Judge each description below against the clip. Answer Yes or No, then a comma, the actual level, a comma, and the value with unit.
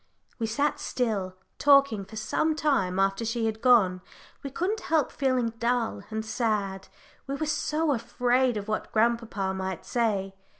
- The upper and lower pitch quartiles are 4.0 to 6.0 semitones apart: Yes, average, 4.6 semitones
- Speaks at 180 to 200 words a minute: No, average, 155 wpm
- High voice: Yes, high, 230 Hz